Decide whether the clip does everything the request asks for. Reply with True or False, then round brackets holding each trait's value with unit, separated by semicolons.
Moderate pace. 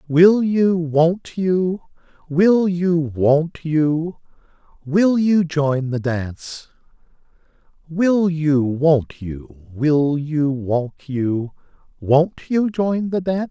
False (115 wpm)